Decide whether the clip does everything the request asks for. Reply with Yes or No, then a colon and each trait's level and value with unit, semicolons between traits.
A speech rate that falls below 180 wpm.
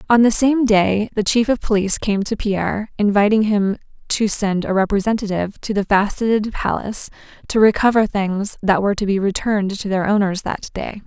No: average, 185 wpm